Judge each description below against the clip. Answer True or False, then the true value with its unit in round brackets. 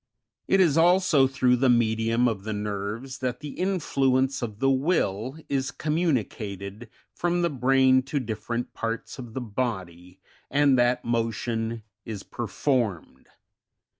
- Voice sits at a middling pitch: False (125 Hz)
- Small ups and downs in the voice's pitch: False (3.6 semitones)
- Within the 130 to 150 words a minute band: True (135 wpm)